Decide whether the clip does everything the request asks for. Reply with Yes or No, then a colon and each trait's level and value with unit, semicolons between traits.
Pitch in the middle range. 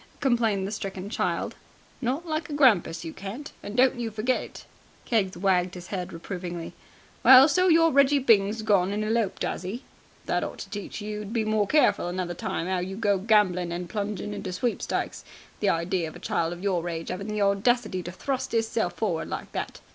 No: high, 205 Hz